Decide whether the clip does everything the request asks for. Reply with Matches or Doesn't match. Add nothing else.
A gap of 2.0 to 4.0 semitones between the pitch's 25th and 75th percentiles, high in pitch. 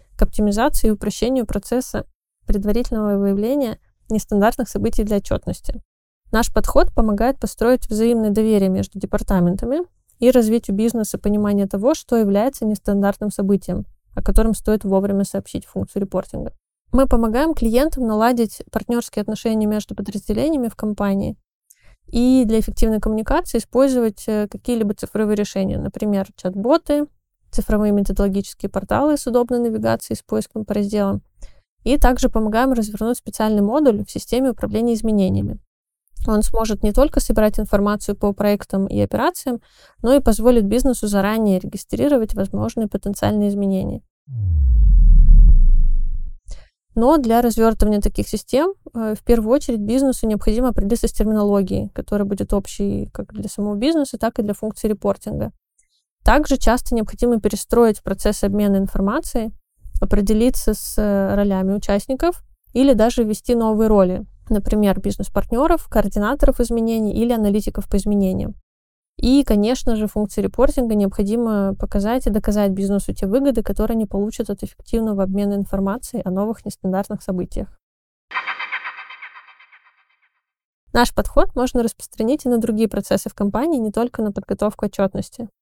Matches